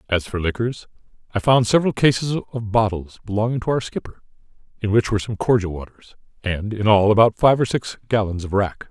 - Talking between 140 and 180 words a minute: No, average, 195 wpm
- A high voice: No, low, 110 Hz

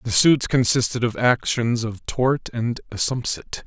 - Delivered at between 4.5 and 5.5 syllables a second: No, 4.1 syllables/s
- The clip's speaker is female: No, male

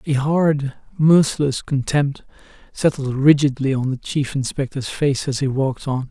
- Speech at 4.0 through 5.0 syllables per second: Yes, 4.4 syllables/s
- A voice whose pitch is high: No, medium, 140 Hz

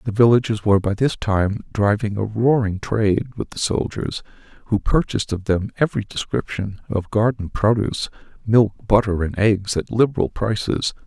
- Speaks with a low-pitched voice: Yes, low, 105 Hz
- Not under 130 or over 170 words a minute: Yes, average, 155 wpm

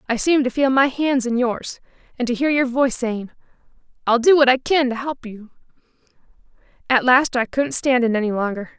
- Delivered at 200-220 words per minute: Yes, fast, 205 wpm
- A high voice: Yes, very high, 250 Hz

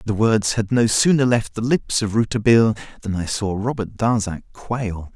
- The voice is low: Yes, low, 110 Hz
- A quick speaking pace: No, average, 185 wpm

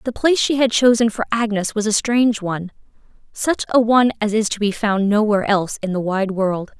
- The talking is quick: Yes, fast, 210 wpm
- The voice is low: No, high, 215 Hz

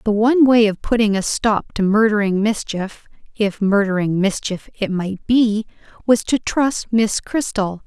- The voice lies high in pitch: Yes, high, 210 Hz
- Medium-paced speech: Yes, average, 160 wpm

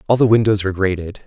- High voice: No, low, 100 Hz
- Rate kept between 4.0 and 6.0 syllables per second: No, 7.3 syllables/s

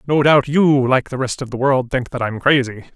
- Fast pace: Yes, fast, 265 wpm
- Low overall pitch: Yes, low, 130 Hz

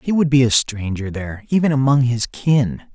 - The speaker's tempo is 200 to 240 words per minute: Yes, fast, 205 wpm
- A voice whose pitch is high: No, low, 125 Hz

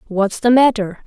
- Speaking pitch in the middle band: No, high, 220 Hz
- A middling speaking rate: Yes, average, 170 wpm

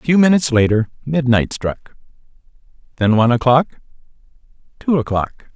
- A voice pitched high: No, low, 130 Hz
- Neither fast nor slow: No, slow, 110 wpm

